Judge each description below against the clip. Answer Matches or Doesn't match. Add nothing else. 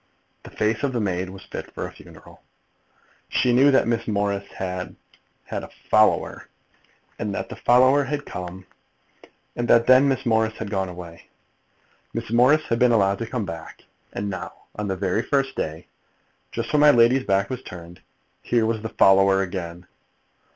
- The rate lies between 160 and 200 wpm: Matches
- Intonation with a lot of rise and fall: Doesn't match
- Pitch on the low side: Matches